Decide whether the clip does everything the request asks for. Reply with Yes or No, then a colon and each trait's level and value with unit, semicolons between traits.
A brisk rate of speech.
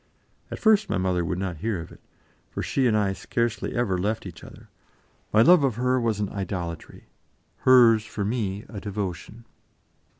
No: average, 175 wpm